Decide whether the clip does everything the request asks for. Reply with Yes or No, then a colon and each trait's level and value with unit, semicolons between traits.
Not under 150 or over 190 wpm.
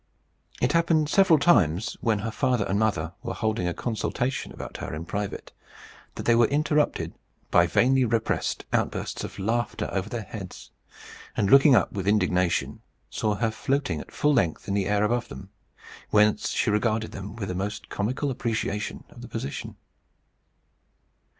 Yes: average, 165 wpm